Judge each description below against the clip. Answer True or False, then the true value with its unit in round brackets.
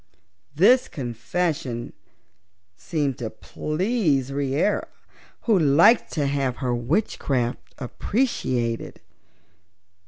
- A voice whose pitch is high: False (140 Hz)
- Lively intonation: True (6.3 semitones)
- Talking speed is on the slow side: True (75 wpm)